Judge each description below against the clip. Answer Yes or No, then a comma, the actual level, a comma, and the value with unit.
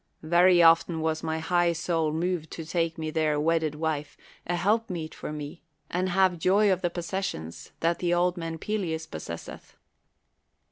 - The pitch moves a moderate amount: No, narrow, 2.0 semitones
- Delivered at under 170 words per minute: No, average, 175 wpm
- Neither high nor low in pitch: Yes, medium, 165 Hz